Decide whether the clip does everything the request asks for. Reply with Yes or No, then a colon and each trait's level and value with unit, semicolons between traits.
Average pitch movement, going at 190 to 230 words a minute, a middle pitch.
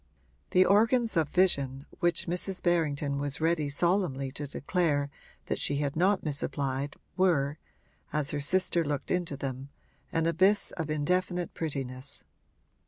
No: average, 4.2 semitones; slow, 135 wpm; medium, 155 Hz